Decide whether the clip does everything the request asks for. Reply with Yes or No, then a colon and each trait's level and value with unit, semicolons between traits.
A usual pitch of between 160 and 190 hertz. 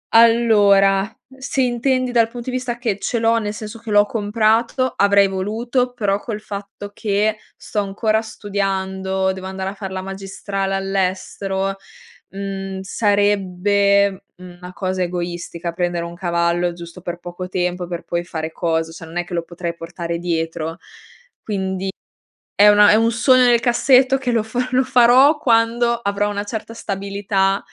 No: high, 200 Hz